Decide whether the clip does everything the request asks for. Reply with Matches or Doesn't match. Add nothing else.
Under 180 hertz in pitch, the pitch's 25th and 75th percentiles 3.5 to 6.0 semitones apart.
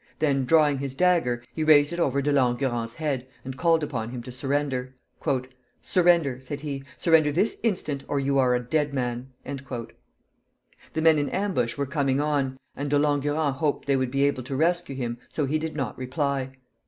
Doesn't match